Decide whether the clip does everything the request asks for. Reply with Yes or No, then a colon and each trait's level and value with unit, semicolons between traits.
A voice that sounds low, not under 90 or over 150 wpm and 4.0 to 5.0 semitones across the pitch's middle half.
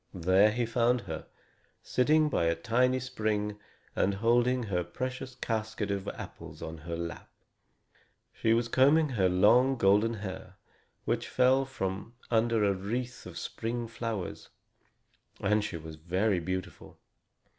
Yes: low, 110 Hz; slow, 135 wpm; average, 4.3 semitones